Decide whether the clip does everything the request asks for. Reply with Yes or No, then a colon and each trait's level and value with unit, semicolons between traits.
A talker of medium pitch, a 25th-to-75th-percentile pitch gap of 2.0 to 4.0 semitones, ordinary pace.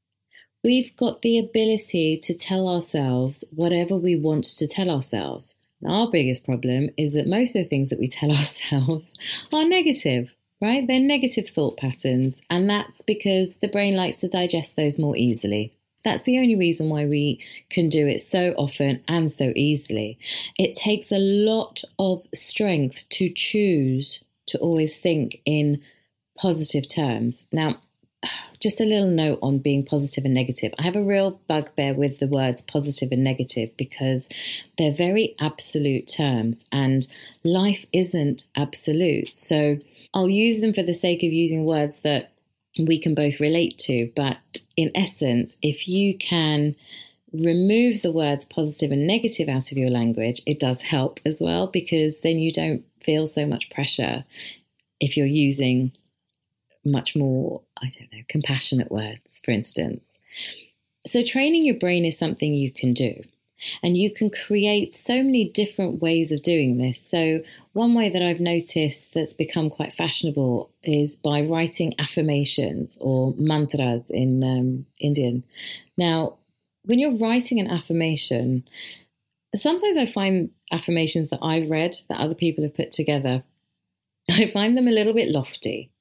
No: medium, 155 Hz; average, 5.1 semitones; average, 155 wpm